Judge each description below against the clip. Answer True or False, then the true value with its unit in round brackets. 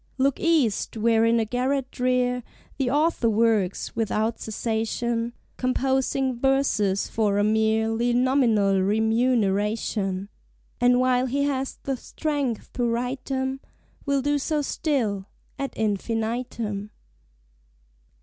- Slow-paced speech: True (115 wpm)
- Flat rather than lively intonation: False (3.2 semitones)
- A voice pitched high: True (240 Hz)